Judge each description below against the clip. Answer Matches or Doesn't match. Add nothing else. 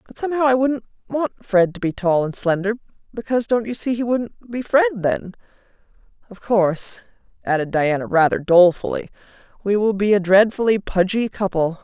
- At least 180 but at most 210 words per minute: Doesn't match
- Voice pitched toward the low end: Doesn't match